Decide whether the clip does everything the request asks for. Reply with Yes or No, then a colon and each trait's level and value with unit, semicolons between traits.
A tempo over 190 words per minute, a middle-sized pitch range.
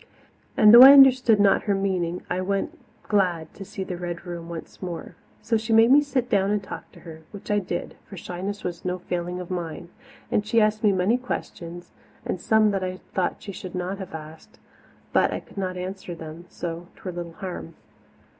Yes: fast, 205 wpm; average, 3.1 semitones